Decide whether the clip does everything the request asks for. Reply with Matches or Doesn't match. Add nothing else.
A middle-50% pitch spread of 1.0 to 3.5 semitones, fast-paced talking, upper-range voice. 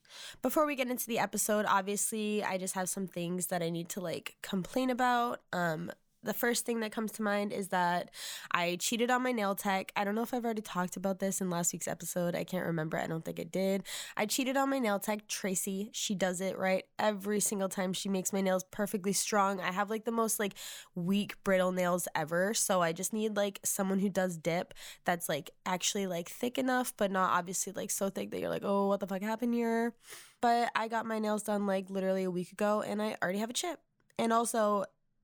Matches